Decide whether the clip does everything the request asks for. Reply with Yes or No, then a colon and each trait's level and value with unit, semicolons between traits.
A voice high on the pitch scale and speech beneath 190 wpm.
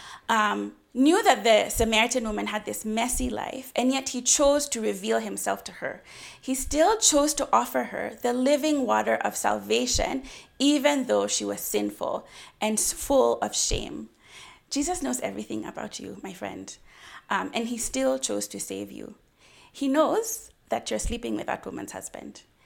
Yes: high, 245 Hz; average, 165 wpm